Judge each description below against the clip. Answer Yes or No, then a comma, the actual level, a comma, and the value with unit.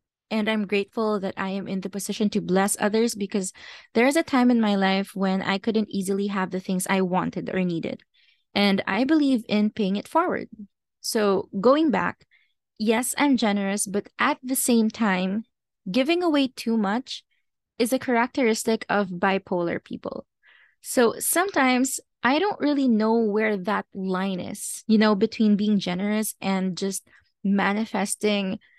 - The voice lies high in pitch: Yes, high, 210 Hz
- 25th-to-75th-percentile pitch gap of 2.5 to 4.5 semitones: Yes, average, 3.5 semitones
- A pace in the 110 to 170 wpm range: Yes, average, 160 wpm